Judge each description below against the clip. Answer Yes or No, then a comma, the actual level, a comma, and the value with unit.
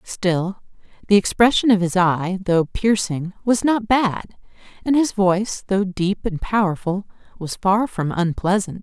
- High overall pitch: Yes, high, 195 Hz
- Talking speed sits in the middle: Yes, average, 150 wpm